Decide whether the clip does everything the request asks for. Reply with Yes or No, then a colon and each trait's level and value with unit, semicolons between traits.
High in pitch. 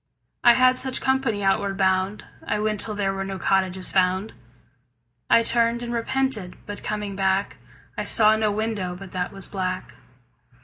Yes: high, 205 Hz